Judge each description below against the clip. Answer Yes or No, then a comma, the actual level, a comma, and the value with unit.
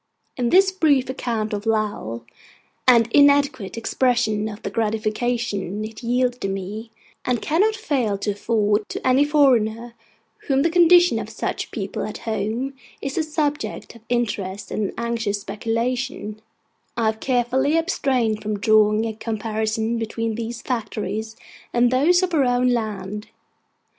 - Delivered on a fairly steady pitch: No, average, 3.4 semitones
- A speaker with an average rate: Yes, average, 145 wpm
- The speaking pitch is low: No, high, 230 Hz